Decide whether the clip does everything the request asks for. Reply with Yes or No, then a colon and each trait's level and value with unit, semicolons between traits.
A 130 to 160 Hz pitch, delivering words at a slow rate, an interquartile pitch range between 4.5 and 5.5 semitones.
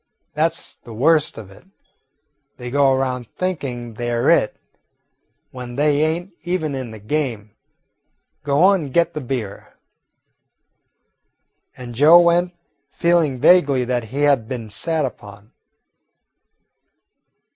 Yes: low, 135 Hz; slow, 125 wpm; average, 4.9 semitones